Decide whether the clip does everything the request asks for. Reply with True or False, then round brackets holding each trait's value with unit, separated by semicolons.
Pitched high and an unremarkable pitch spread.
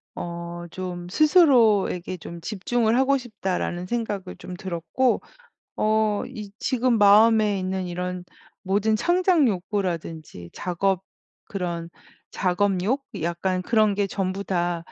True (195 Hz; 3.6 semitones)